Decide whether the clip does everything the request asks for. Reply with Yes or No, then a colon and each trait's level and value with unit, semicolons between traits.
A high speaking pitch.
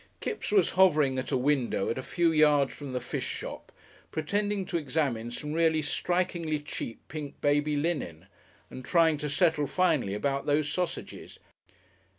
No: medium, 150 Hz